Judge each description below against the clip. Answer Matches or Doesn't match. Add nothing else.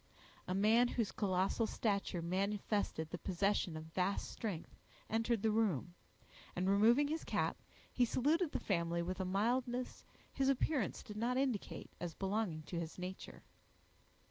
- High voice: Matches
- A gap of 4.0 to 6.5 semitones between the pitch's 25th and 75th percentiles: Matches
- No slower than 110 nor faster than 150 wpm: Matches